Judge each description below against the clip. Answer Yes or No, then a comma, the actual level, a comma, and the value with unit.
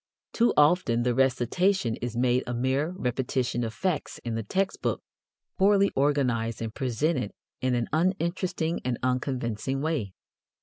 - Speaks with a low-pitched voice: Yes, low, 130 Hz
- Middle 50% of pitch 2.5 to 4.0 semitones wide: No, average, 5.3 semitones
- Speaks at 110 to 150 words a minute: Yes, average, 140 wpm